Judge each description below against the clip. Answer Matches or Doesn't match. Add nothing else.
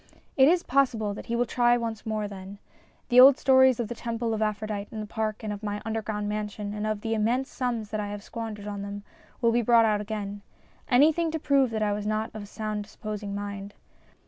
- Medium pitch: Doesn't match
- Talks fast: Matches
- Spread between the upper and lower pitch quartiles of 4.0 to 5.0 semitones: Doesn't match